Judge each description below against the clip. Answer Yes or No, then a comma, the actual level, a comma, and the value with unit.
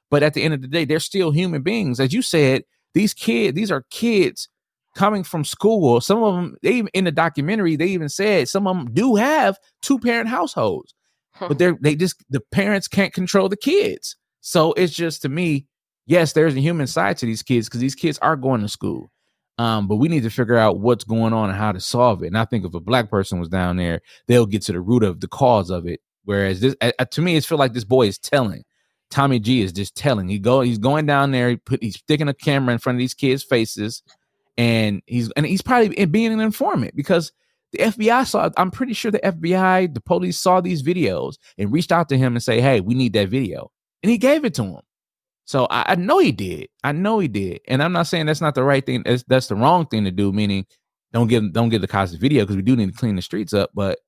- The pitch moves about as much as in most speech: No, wide, 7.9 semitones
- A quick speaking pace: Yes, fast, 250 wpm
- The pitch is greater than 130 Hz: Yes, medium, 140 Hz